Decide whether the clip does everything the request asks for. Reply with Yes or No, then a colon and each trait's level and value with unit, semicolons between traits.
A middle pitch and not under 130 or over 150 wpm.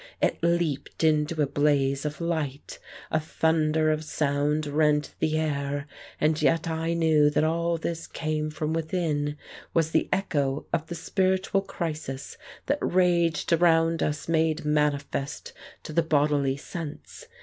Yes: medium, 155 Hz; average, 140 wpm